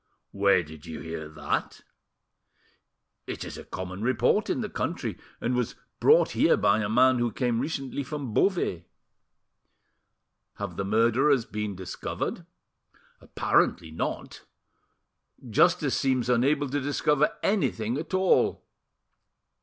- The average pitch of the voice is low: Yes, low, 120 Hz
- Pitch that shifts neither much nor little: No, wide, 5.8 semitones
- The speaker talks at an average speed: No, slow, 120 wpm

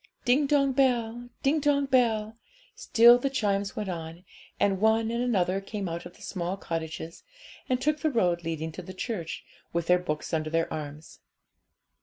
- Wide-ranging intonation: Yes, wide, 6.3 semitones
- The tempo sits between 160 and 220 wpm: Yes, average, 175 wpm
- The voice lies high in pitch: Yes, high, 200 Hz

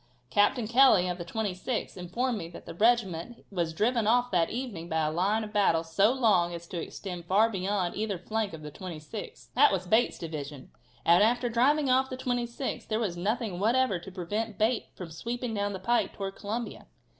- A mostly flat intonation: No, average, 5.2 semitones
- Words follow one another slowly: No, average, 195 wpm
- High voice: Yes, high, 205 Hz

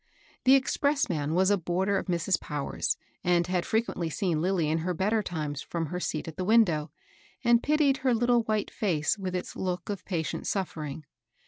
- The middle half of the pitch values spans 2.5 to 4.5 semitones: No, average, 4.9 semitones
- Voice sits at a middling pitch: Yes, medium, 180 Hz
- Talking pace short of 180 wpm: No, average, 185 wpm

